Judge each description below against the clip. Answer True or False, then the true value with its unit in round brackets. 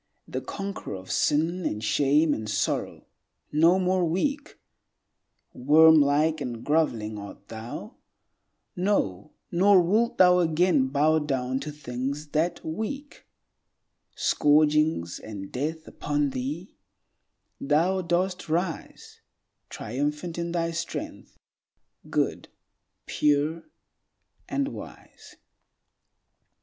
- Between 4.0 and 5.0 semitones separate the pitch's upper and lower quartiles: True (4.3 semitones)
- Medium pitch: True (155 Hz)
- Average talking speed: False (95 wpm)